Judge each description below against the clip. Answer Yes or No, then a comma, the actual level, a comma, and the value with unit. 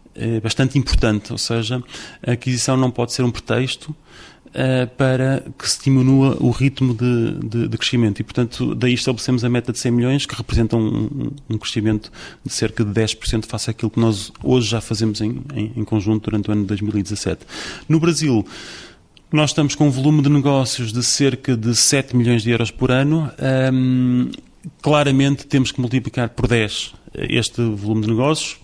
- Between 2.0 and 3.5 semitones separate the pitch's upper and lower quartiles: Yes, average, 3.1 semitones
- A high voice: No, low, 125 Hz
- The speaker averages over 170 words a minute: Yes, average, 180 wpm